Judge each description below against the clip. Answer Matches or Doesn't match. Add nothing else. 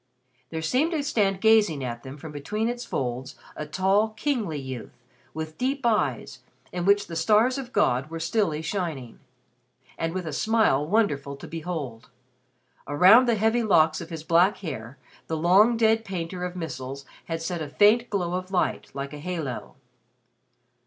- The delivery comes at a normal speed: Matches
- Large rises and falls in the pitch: Matches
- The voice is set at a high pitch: Doesn't match